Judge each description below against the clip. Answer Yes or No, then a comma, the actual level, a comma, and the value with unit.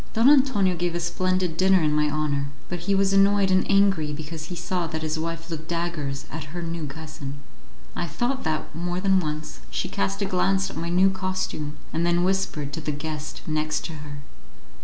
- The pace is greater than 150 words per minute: Yes, average, 200 wpm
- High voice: No, medium, 165 Hz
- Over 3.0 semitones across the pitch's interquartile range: Yes, average, 3.5 semitones